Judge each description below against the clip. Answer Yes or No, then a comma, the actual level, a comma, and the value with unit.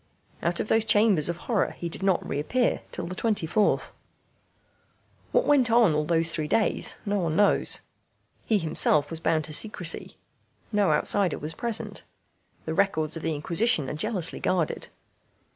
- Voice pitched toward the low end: No, medium, 175 Hz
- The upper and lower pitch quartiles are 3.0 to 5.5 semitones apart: Yes, average, 5.0 semitones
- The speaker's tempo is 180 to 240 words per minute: No, average, 160 wpm